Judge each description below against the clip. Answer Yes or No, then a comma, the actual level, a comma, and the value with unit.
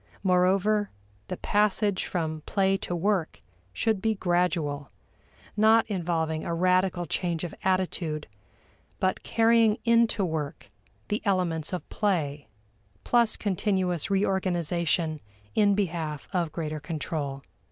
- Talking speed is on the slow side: Yes, slow, 110 wpm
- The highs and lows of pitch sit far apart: No, average, 3.9 semitones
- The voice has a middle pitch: Yes, medium, 180 Hz